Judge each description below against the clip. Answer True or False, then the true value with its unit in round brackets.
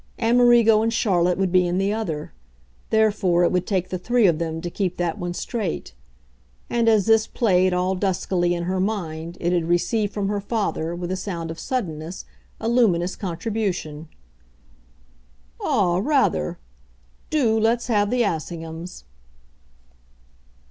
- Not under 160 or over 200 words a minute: False (150 wpm)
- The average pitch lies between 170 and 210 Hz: True (185 Hz)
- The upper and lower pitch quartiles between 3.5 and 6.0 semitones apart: True (4.1 semitones)